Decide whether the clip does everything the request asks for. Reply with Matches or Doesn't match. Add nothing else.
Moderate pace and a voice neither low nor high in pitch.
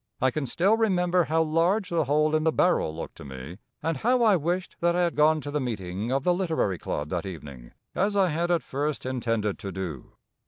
Doesn't match